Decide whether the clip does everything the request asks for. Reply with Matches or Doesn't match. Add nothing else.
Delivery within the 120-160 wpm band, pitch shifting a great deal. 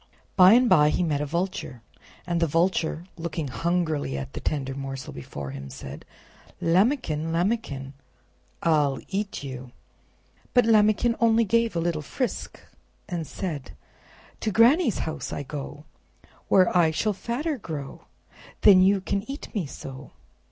Matches